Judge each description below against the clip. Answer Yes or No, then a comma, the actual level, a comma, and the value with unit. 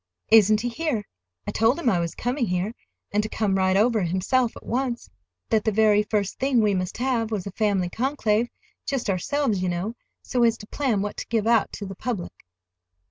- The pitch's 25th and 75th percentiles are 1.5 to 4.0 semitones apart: Yes, average, 3.5 semitones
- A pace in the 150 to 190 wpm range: No, fast, 205 wpm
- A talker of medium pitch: No, high, 215 Hz